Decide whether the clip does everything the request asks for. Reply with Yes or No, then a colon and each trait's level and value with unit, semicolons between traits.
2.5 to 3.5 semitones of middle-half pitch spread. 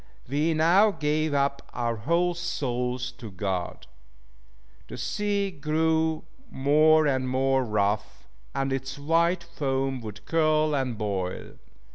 No: average, 4.3 semitones